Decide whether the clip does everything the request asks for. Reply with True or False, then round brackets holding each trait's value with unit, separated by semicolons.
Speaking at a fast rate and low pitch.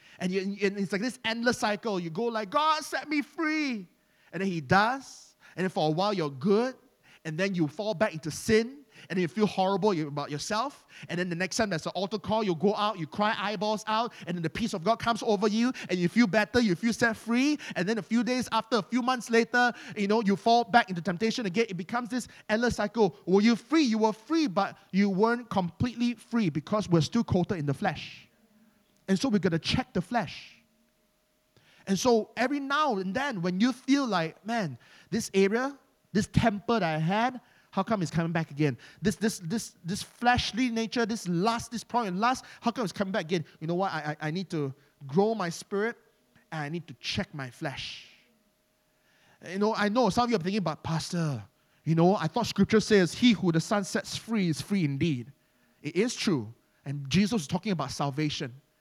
False (220 wpm; 205 Hz)